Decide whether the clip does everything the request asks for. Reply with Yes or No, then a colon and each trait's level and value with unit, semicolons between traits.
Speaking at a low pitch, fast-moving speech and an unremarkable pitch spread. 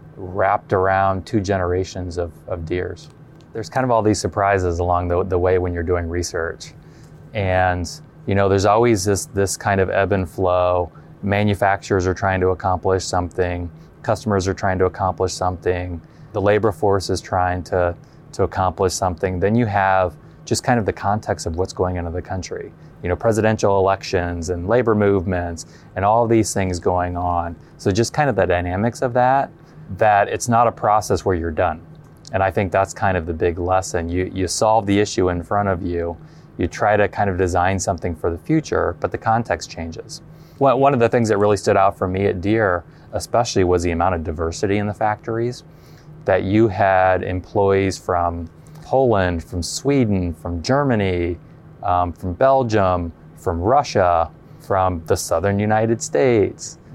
No: very low, 95 Hz; average, 180 wpm; average, 3.5 semitones